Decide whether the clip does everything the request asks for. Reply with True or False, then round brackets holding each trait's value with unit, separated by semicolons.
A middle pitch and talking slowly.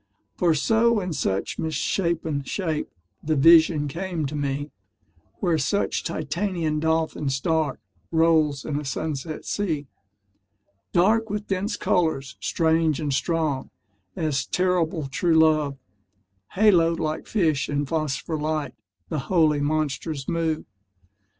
True (160 Hz; 120 wpm)